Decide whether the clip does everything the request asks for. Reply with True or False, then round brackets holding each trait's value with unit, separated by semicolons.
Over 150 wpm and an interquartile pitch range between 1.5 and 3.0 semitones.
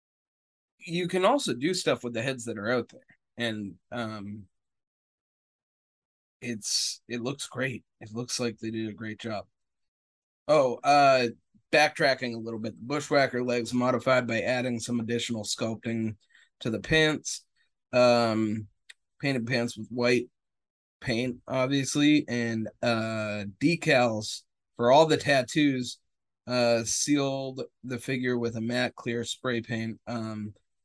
False (135 wpm; 2.4 semitones)